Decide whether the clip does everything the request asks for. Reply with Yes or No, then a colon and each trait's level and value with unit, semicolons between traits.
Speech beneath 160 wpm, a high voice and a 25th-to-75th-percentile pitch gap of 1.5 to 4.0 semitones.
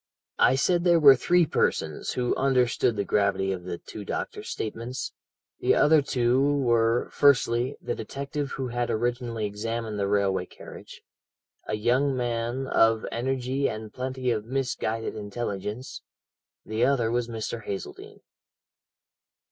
No: slow, 135 wpm; low, 120 Hz; average, 3.4 semitones